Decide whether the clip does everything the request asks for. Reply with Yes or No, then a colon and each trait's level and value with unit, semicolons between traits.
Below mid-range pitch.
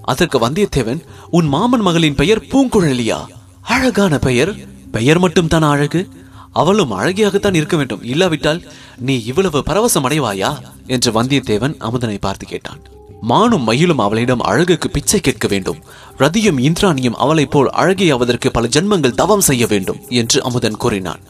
No: medium, 145 Hz